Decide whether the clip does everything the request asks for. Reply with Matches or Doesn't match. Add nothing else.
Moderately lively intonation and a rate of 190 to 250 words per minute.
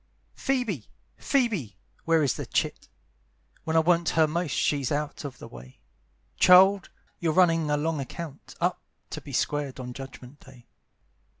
Doesn't match